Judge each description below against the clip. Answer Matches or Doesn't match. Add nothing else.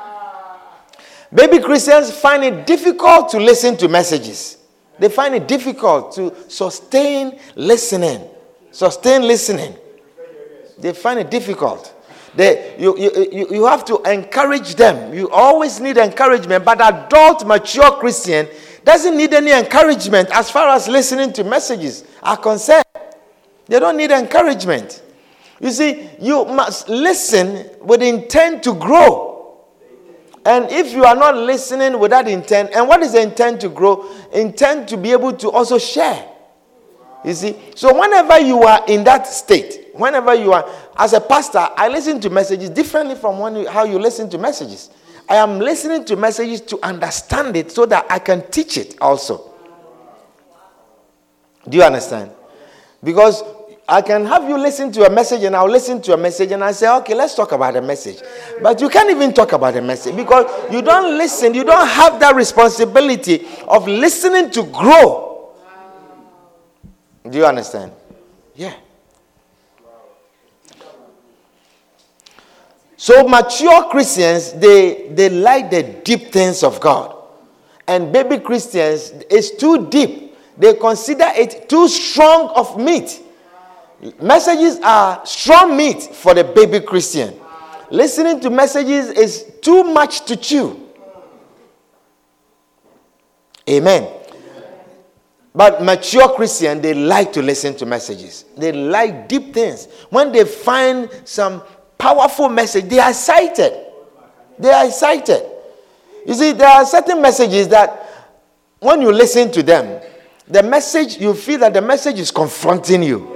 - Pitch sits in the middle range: Doesn't match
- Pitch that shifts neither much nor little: Doesn't match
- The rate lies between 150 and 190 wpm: Doesn't match